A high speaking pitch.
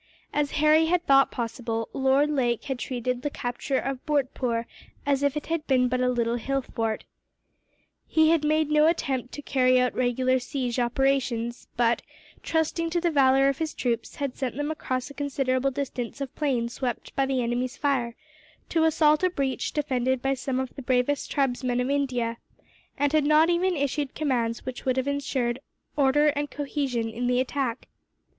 Yes: very high, 270 Hz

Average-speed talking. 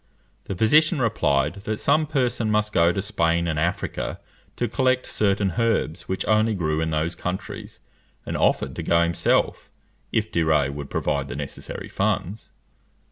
Yes: average, 160 wpm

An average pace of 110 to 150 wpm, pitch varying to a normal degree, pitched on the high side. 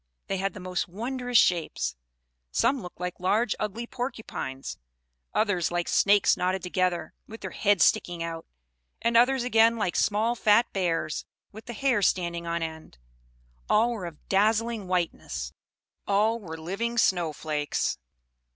Yes: average, 145 wpm; average, 4.8 semitones; high, 195 Hz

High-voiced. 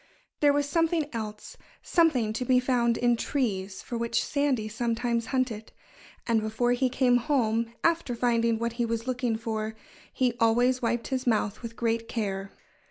Yes: high, 235 Hz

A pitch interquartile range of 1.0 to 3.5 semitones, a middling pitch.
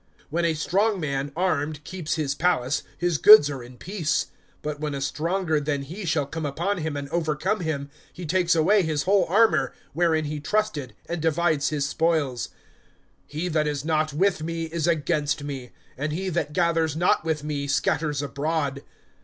Yes: average, 2.9 semitones; medium, 155 Hz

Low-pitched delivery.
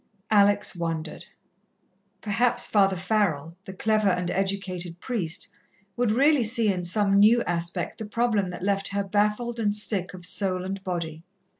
No: high, 200 Hz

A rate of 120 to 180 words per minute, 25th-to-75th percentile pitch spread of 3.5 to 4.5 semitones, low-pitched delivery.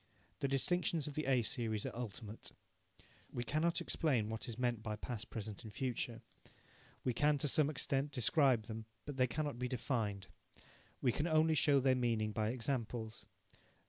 Yes: average, 170 wpm; average, 4.2 semitones; low, 125 Hz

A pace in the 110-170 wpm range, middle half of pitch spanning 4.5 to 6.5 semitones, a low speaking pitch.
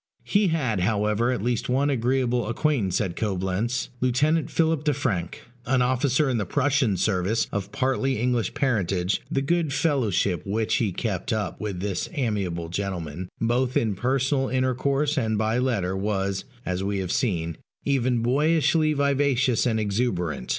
Yes: average, 155 wpm; average, 5.3 semitones; low, 120 Hz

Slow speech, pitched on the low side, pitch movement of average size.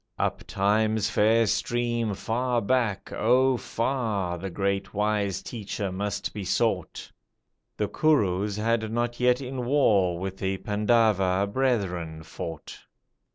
Yes: slow, 120 wpm; low, 105 Hz; average, 3.5 semitones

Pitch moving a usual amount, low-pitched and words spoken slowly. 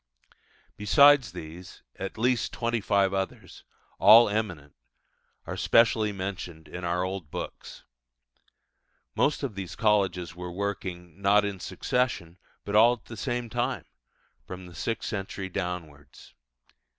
Yes: average, 3.9 semitones; low, 100 Hz; slow, 125 wpm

